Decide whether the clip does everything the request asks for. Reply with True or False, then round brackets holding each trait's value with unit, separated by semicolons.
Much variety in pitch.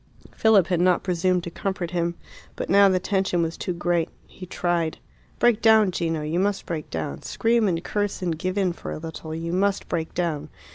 False (2.8 semitones)